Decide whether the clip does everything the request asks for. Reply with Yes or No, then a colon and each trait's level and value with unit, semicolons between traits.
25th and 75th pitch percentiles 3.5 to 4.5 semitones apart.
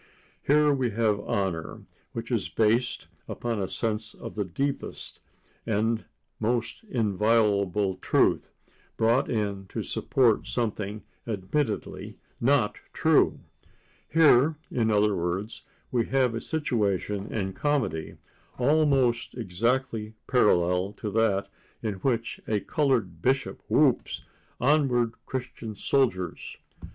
Yes: average, 3.8 semitones